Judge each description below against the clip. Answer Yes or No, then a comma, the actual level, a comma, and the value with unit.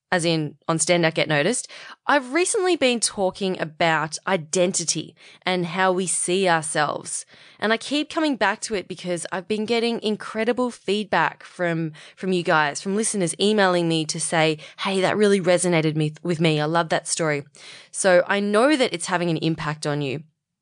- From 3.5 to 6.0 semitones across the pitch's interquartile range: Yes, average, 4.0 semitones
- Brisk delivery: No, average, 180 wpm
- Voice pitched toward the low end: No, medium, 180 Hz